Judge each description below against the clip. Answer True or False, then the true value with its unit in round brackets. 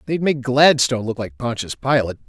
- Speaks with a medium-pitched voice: False (125 Hz)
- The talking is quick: False (185 wpm)